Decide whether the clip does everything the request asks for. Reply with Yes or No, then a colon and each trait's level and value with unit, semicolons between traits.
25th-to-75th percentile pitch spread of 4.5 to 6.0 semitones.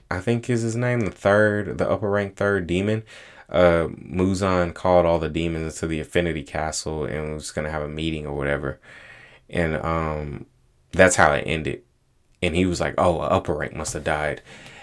No: average, 3.7 semitones